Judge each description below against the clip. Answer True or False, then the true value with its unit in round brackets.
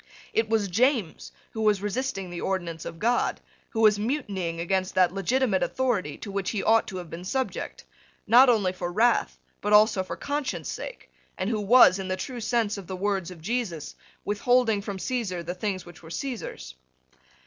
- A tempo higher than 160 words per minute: True (185 wpm)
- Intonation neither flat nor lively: True (4.1 semitones)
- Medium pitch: False (205 Hz)